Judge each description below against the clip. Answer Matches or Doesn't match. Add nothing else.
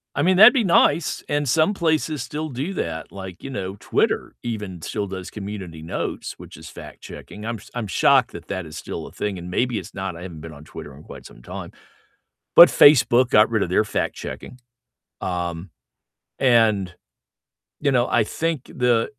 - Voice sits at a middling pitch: Doesn't match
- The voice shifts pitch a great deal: Matches